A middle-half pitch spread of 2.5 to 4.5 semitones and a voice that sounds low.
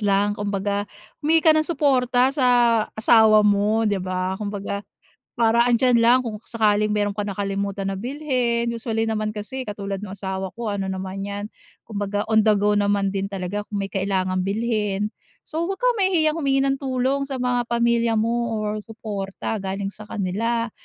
No: average, 3.0 semitones; high, 215 Hz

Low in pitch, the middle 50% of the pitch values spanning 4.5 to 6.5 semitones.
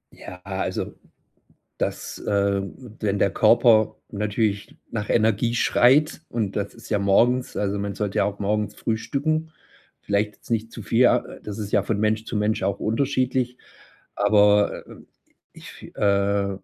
No: low, 105 Hz; narrow, 2.5 semitones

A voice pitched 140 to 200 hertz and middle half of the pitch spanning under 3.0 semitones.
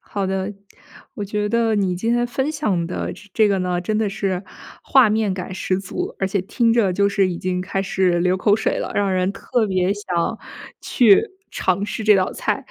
Yes: high, 195 Hz; narrow, 2.6 semitones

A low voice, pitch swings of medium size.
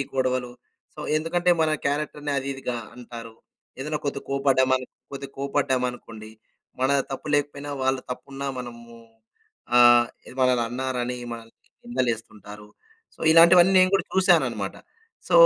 Yes: low, 130 Hz; average, 3.1 semitones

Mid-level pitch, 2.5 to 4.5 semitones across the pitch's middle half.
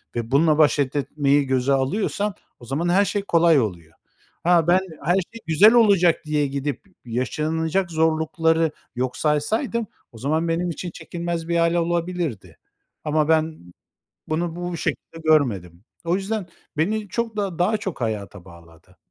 Yes: medium, 160 Hz; average, 4.2 semitones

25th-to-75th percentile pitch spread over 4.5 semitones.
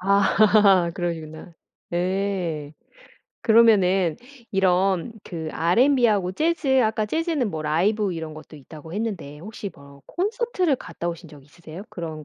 Yes: average, 5.2 semitones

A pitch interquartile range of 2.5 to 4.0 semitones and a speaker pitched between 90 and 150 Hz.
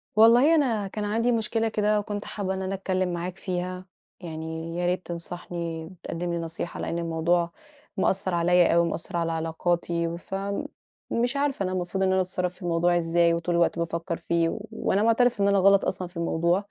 No: average, 2.8 semitones; medium, 180 Hz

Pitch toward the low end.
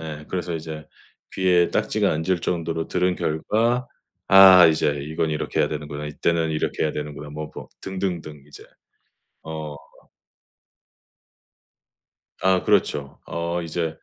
Yes: very low, 80 Hz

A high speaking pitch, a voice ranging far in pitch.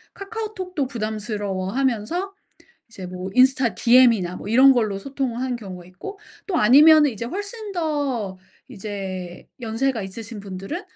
Yes: high, 235 Hz; wide, 6.4 semitones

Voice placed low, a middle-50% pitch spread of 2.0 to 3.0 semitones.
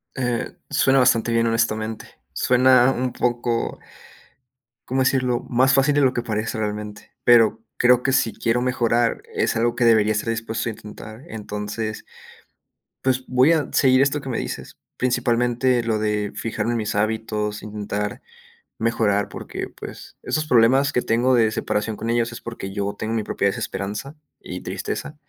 Yes: low, 115 Hz; average, 2.7 semitones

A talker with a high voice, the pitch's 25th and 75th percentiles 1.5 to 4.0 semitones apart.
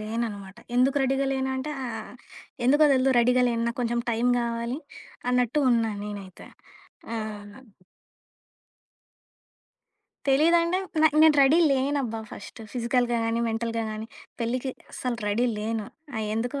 Yes: high, 240 Hz; average, 2.9 semitones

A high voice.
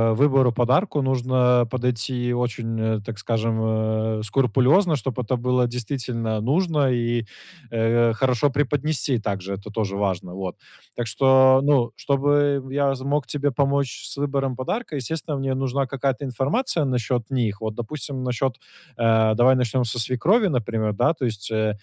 No: low, 125 Hz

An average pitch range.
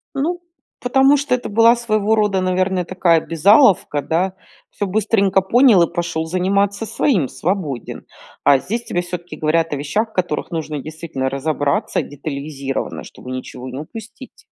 No: wide, 5.9 semitones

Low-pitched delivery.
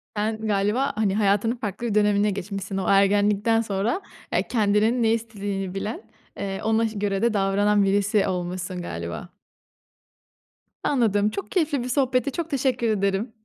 No: high, 210 Hz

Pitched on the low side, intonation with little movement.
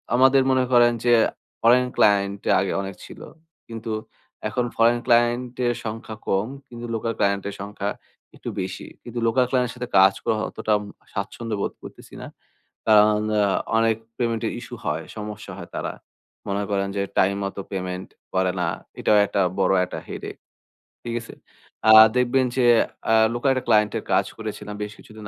No: low, 110 Hz; average, 3.1 semitones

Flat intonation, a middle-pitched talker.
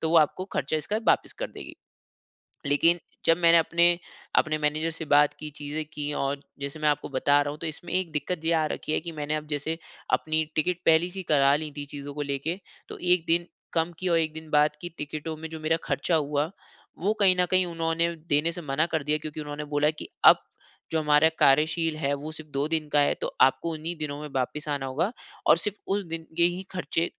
Yes: narrow, 2.1 semitones; medium, 155 Hz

